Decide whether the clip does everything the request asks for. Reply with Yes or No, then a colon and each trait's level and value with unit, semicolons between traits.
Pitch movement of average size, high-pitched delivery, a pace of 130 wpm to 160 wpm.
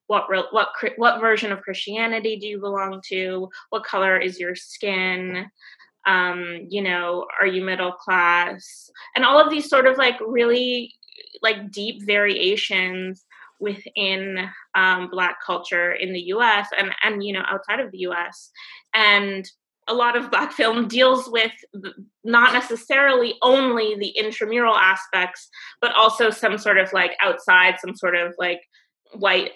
Yes: average, 3.7 semitones; high, 205 Hz; average, 150 wpm